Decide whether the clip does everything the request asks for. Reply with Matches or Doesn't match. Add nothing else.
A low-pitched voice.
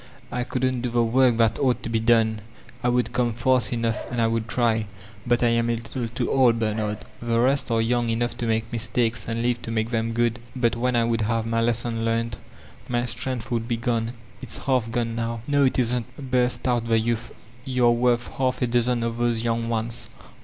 Matches